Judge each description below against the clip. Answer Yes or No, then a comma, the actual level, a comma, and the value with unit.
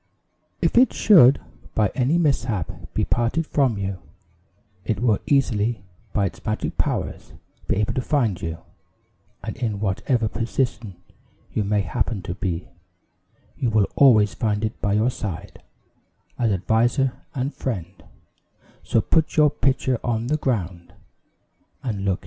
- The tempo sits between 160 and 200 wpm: No, average, 145 wpm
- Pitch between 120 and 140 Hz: No, low, 110 Hz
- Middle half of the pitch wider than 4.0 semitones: Yes, average, 4.5 semitones